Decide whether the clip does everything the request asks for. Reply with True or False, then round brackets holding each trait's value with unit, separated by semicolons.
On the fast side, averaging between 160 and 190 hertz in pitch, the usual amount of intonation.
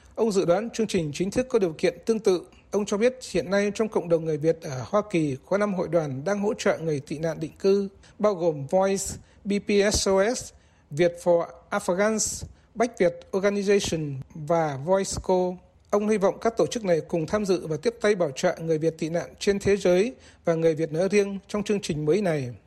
False (215 wpm; 185 Hz; 3.8 semitones)